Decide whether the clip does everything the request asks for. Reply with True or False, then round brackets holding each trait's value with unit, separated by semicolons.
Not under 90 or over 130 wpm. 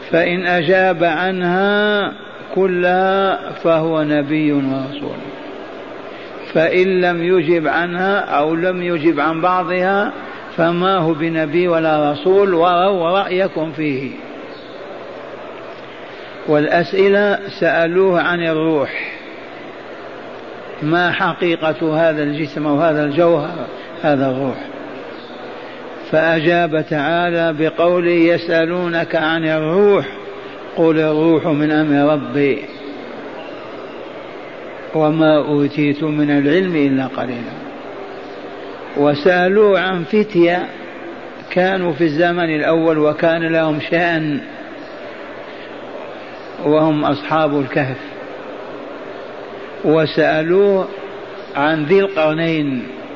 False (80 wpm)